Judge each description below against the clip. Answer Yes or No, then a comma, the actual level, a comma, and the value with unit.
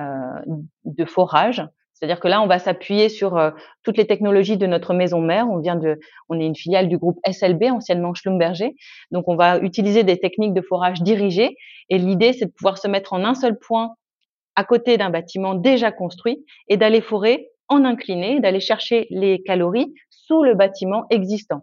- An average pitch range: Yes, average, 4.1 semitones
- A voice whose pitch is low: No, high, 195 Hz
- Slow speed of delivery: No, average, 190 wpm